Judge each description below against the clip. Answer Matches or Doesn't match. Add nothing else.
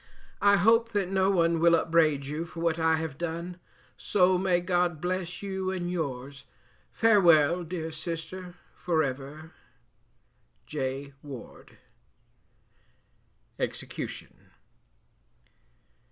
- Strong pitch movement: Doesn't match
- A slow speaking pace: Matches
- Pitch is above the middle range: Doesn't match